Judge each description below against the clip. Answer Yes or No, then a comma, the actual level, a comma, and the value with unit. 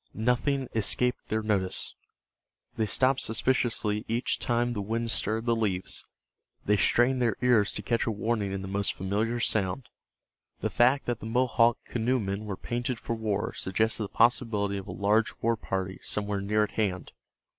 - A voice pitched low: Yes, low, 110 Hz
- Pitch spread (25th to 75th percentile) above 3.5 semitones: No, average, 2.8 semitones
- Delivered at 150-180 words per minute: Yes, average, 165 wpm